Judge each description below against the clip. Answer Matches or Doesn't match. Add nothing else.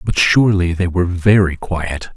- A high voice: Doesn't match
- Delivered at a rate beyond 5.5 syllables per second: Doesn't match